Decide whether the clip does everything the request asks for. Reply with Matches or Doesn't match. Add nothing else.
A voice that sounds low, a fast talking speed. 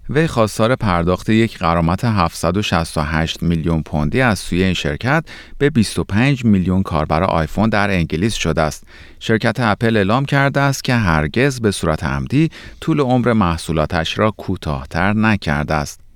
Doesn't match